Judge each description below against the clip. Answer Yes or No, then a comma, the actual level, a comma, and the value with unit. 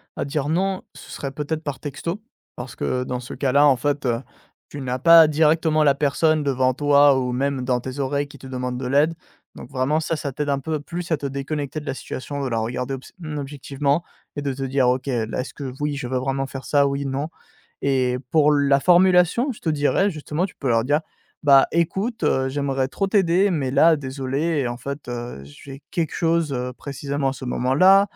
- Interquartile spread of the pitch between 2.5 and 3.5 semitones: Yes, average, 2.9 semitones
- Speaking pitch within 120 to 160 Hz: Yes, medium, 140 Hz